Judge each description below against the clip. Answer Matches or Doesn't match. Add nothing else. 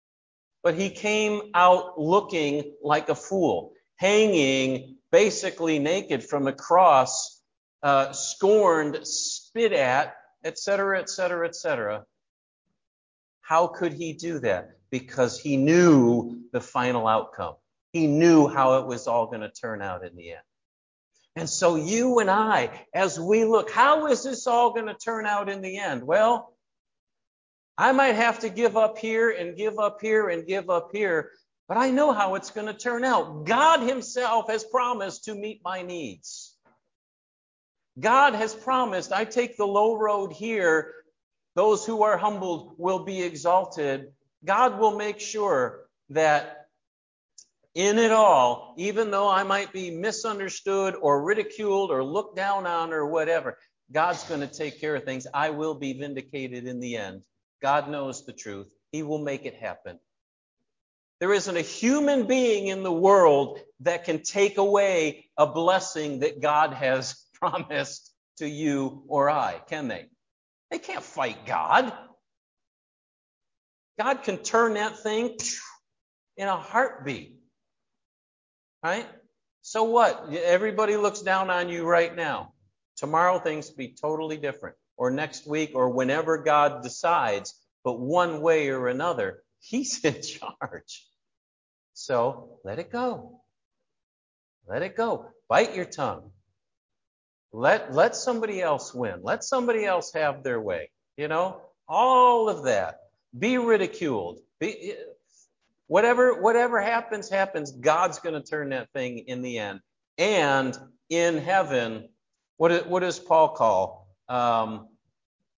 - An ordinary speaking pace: Matches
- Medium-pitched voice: Matches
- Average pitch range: Doesn't match